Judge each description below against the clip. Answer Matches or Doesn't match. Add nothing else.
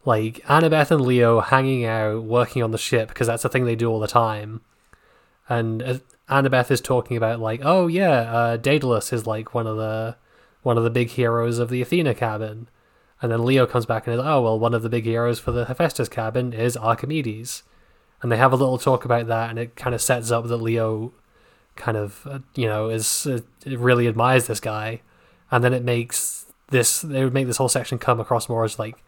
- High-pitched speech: Doesn't match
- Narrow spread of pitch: Matches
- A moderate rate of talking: Doesn't match